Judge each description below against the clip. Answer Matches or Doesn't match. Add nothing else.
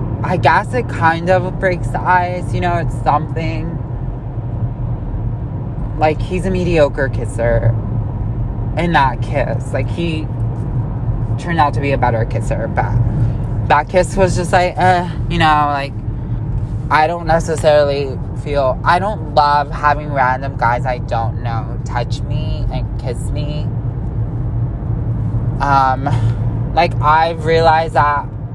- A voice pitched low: Matches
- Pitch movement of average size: Matches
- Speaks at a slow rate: Matches